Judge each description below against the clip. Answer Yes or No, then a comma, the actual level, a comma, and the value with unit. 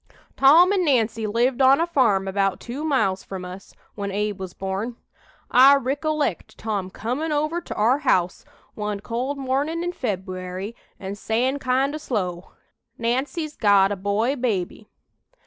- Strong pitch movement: Yes, wide, 5.9 semitones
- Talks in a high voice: Yes, high, 235 Hz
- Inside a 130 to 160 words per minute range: Yes, average, 150 wpm